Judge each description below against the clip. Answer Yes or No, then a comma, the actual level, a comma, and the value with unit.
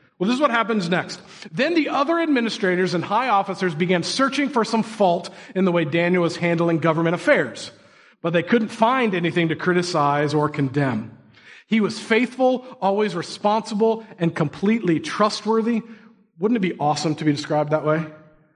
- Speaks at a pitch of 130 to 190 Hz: Yes, medium, 185 Hz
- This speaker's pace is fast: No, average, 170 wpm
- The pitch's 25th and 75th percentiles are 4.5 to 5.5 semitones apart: Yes, average, 5.2 semitones